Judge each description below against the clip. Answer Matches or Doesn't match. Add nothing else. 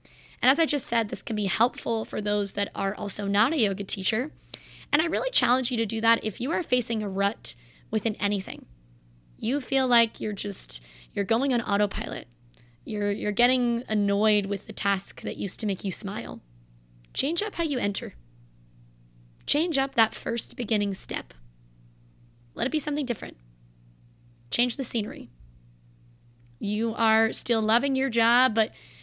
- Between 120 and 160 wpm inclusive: Doesn't match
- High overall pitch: Matches